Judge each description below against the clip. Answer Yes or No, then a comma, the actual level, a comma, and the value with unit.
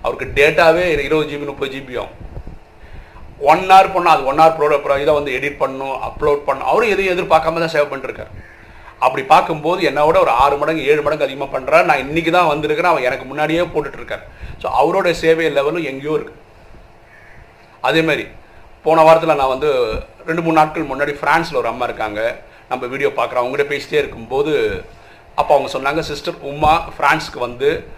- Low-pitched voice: No, medium, 155 Hz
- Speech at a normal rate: No, fast, 160 wpm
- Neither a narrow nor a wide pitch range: Yes, average, 3.9 semitones